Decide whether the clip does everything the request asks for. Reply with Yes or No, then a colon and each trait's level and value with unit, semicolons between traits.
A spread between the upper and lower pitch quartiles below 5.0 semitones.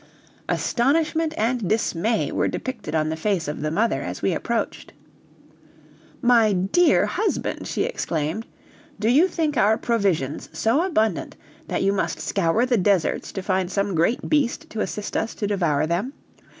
No: wide, 5.4 semitones